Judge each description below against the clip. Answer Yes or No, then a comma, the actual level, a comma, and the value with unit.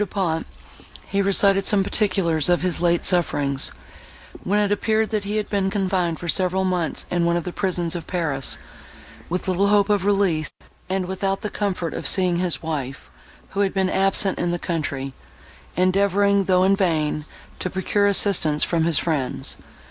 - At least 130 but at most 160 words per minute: No, average, 175 wpm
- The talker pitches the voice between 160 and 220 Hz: Yes, medium, 185 Hz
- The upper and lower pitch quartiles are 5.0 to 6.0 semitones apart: No, average, 2.8 semitones